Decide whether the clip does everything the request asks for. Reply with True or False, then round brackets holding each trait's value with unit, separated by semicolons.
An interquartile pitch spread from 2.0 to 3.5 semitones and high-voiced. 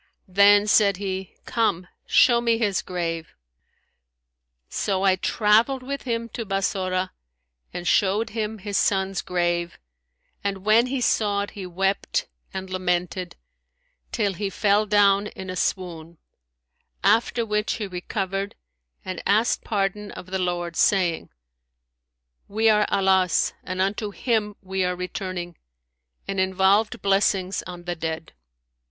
True (2.4 semitones; 195 Hz)